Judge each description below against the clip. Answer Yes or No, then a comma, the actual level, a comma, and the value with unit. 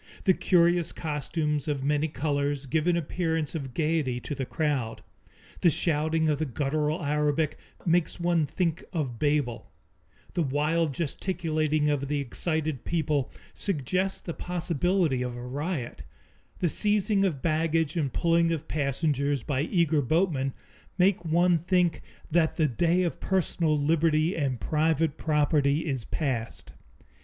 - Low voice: No, medium, 155 Hz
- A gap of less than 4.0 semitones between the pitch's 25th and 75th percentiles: Yes, average, 2.9 semitones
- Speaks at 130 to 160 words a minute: Yes, average, 140 wpm